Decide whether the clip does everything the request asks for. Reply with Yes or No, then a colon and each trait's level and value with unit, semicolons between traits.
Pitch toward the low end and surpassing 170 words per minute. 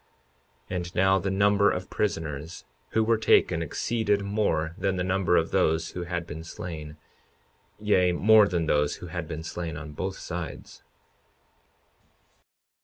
No: very low, 90 Hz; average, 150 wpm